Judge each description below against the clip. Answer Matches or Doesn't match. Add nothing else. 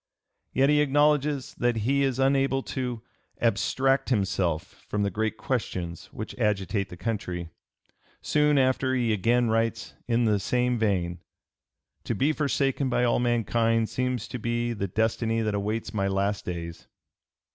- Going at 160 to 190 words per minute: Doesn't match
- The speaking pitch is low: Matches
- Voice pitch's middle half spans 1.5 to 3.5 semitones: Doesn't match